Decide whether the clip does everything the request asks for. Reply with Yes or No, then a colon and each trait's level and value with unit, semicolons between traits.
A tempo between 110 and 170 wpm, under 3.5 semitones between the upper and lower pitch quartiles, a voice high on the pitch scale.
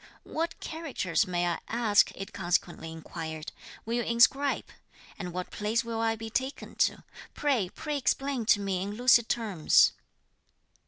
No: average, 150 wpm; average, 5.3 semitones; high, 220 Hz